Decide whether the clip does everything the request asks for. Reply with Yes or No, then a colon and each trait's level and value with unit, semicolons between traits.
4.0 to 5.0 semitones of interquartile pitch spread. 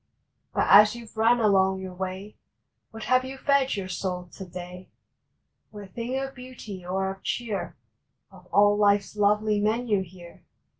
No: average, 3.4 semitones